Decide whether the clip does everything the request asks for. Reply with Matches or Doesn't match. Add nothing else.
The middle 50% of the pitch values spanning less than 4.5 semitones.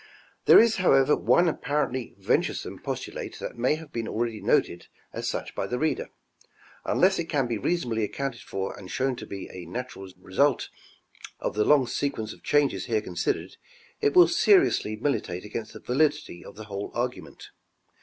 Doesn't match